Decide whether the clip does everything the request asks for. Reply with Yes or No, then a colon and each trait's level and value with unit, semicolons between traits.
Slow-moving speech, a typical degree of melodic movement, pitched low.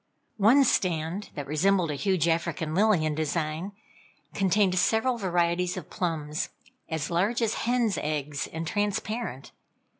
No: slow, 130 wpm; average, 4.7 semitones; medium, 175 Hz